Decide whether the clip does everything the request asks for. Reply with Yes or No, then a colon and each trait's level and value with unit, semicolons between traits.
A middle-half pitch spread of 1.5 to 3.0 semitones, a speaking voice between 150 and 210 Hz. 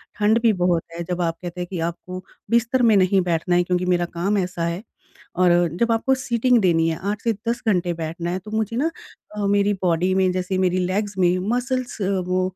No: average, 3.4 semitones; medium, 185 Hz